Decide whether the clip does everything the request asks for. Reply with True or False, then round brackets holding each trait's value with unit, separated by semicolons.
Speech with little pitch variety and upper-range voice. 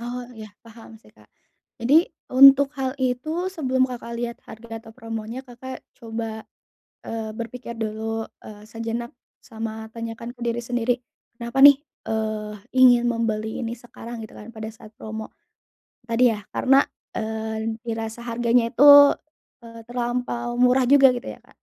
True (1.9 semitones; 235 Hz)